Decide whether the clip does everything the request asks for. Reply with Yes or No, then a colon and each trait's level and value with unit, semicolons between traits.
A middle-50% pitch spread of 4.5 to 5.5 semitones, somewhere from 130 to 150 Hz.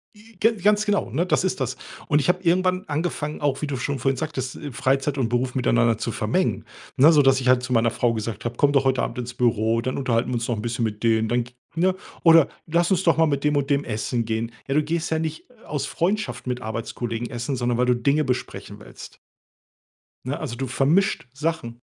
Yes: average, 4.9 semitones; low, 135 Hz